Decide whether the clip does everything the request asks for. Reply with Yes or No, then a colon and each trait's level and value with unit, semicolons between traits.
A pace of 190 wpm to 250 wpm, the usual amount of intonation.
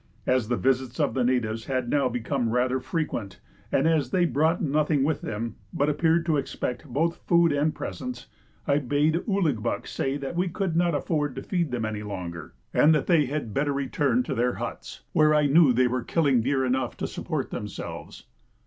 Yes: average, 195 wpm; average, 4.1 semitones